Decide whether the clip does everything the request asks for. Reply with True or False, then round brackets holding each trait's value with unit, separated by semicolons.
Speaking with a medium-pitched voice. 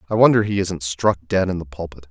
False (90 Hz)